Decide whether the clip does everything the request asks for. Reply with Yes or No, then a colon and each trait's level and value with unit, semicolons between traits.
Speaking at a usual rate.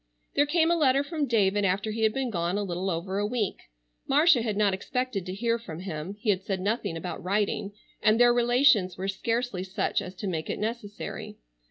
No: fast, 210 wpm